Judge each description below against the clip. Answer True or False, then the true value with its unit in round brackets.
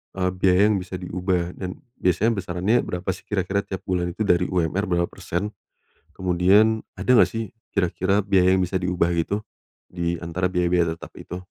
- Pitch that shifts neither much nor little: False (1.8 semitones)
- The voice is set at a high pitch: False (90 Hz)